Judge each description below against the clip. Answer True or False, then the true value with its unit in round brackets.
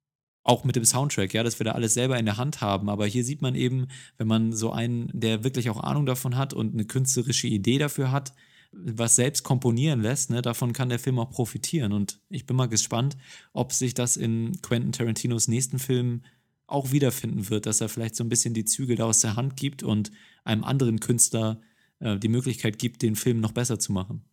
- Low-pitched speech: True (120 Hz)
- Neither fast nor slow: False (220 wpm)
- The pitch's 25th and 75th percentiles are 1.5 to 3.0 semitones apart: True (2.6 semitones)